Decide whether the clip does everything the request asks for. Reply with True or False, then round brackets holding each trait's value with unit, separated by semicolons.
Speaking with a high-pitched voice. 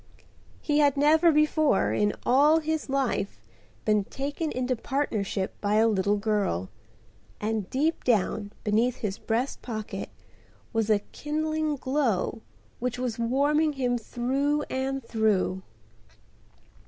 True (250 Hz)